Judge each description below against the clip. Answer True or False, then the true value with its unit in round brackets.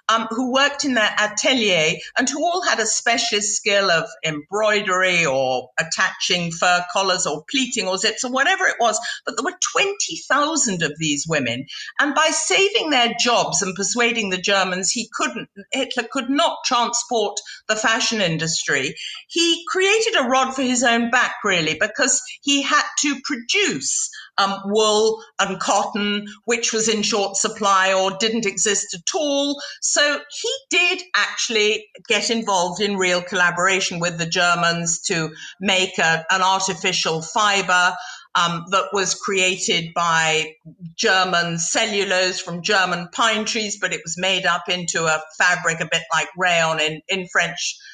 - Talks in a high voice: True (205 Hz)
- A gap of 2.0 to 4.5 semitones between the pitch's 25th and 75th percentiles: False (5.3 semitones)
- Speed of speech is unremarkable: True (155 wpm)